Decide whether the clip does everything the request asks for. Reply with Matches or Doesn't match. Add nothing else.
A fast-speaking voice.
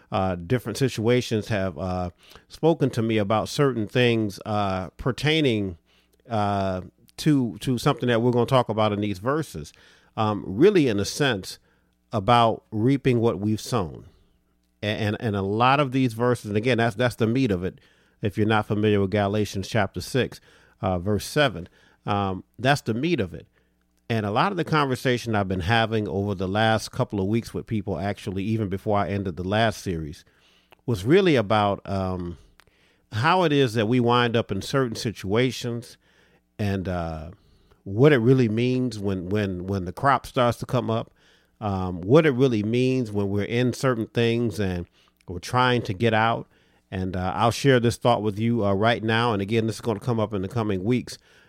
Doesn't match